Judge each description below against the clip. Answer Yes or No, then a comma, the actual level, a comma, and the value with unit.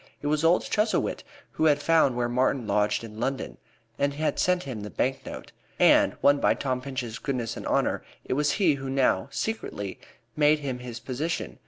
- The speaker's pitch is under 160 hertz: Yes, low, 135 Hz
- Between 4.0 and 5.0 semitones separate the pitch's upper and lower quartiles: No, average, 3.5 semitones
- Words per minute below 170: No, average, 190 wpm